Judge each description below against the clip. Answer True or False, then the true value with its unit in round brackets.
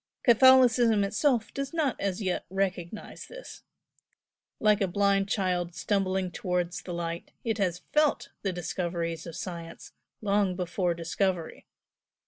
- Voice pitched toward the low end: False (190 Hz)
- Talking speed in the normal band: False (125 wpm)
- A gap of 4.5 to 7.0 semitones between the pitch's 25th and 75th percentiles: False (3.5 semitones)